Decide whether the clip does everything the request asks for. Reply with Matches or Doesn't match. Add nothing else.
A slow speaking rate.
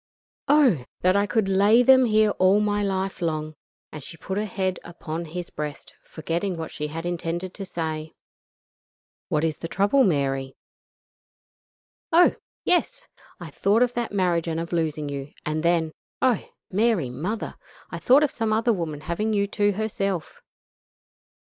Doesn't match